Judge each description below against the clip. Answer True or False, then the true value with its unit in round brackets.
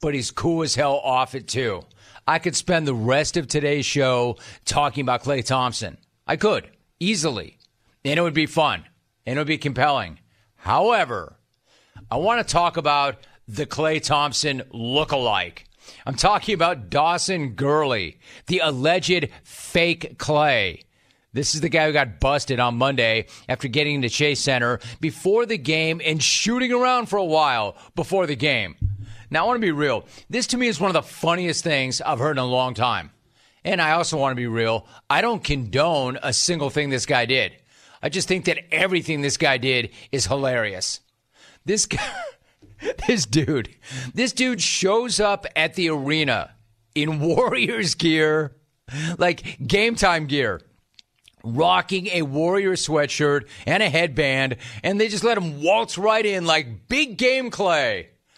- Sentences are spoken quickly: False (165 wpm)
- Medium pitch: True (150 Hz)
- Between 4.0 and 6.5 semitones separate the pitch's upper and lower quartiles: True (5.0 semitones)